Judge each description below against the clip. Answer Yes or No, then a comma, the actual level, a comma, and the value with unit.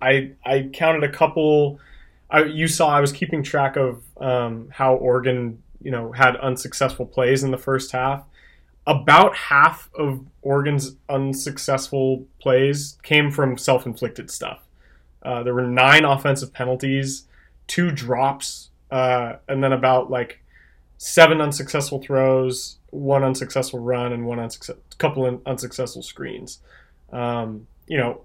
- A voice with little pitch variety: Yes, narrow, 1.9 semitones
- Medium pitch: No, low, 130 Hz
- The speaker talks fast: No, slow, 135 wpm